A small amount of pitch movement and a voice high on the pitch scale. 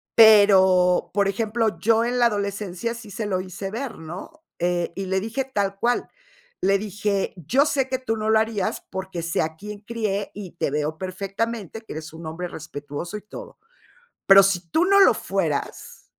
No: average, 3.7 semitones; high, 200 Hz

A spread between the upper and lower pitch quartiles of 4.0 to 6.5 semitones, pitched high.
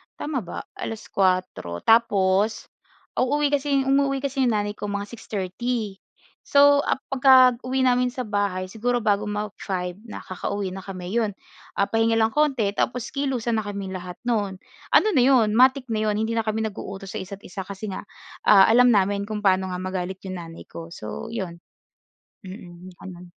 Yes: average, 4.5 semitones; high, 210 Hz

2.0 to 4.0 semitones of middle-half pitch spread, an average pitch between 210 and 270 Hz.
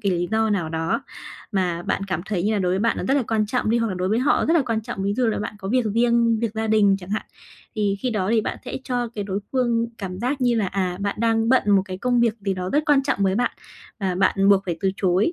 Yes: average, 3.5 semitones; high, 215 Hz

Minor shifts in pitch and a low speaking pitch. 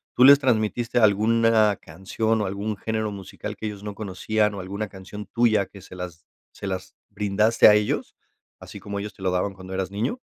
Yes: narrow, 2.2 semitones; low, 105 Hz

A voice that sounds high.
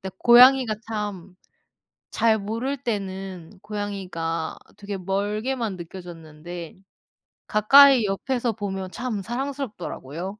Yes: high, 205 Hz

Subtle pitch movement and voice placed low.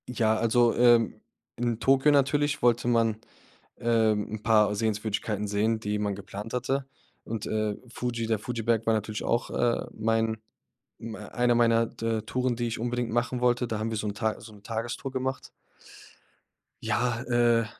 Yes: narrow, 1.9 semitones; low, 115 Hz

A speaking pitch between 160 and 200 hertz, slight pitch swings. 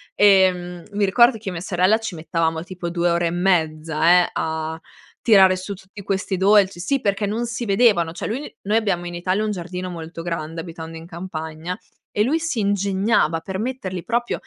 No: medium, 185 Hz; average, 3.4 semitones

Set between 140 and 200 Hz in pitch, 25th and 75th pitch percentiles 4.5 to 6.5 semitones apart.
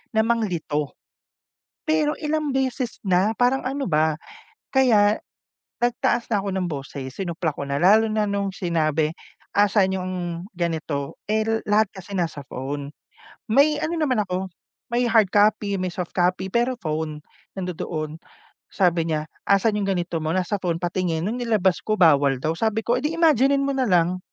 Yes: high, 190 Hz; wide, 5.6 semitones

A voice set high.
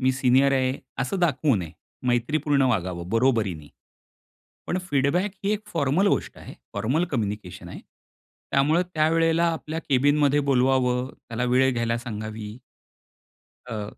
No: low, 130 Hz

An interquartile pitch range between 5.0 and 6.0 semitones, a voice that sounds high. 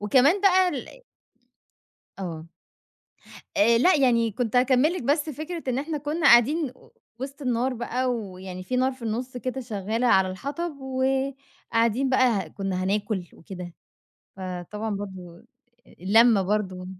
Yes: wide, 5.4 semitones; high, 240 Hz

